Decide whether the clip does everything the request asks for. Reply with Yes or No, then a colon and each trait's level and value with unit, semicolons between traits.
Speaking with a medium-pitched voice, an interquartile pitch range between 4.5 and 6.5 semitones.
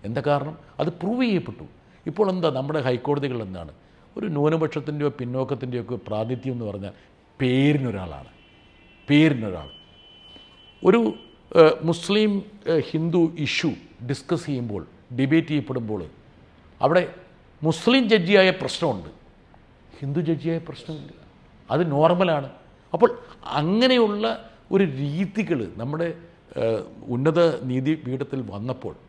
Yes: medium, 145 Hz; average, 5.2 semitones